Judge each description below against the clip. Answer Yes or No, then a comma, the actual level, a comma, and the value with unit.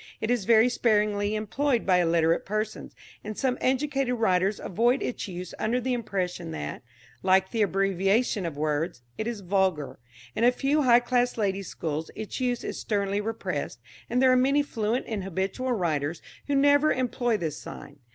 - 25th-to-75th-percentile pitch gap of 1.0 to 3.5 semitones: No, average, 4.9 semitones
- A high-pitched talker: Yes, high, 215 Hz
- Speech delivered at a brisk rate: No, average, 170 wpm